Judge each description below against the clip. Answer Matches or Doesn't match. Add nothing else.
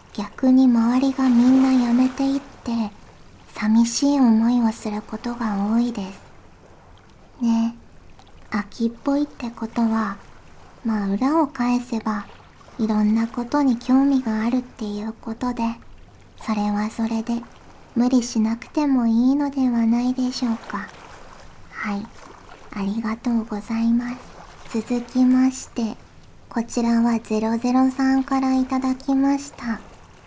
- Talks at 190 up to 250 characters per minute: Matches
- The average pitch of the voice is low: Doesn't match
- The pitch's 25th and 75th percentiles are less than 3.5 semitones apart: Matches